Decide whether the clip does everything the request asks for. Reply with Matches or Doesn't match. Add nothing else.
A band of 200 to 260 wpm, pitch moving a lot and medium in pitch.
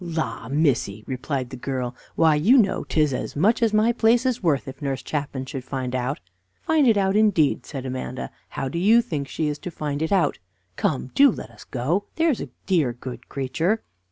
Matches